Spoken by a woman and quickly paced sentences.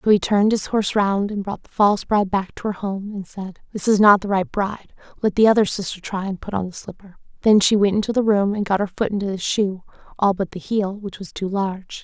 Yes: female; fast, 270 wpm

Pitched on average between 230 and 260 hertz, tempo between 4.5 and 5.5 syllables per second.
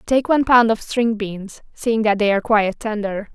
No: high, 220 Hz; 5.2 syllables/s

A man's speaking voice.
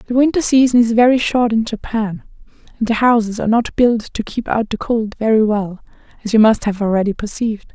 No: female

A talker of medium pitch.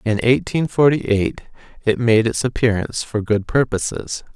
No: low, 115 Hz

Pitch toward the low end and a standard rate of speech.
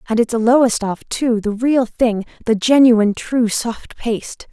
No: high, 230 Hz; average, 160 wpm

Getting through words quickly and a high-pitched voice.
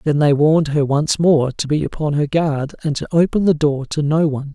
No: fast, 250 wpm; medium, 150 Hz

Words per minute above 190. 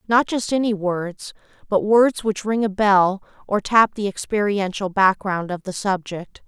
No: average, 165 wpm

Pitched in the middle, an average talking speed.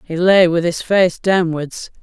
Yes: medium, 175 Hz; average, 180 wpm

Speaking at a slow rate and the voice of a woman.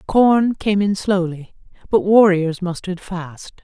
Yes: slow, 130 wpm; female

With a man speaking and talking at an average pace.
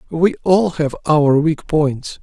Yes: male; average, 160 wpm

